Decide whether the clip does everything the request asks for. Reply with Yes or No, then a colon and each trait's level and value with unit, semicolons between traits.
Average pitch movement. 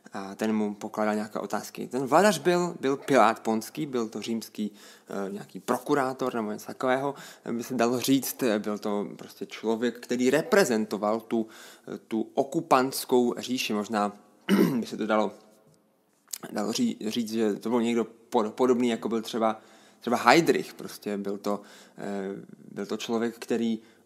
Yes: average, 3.2 semitones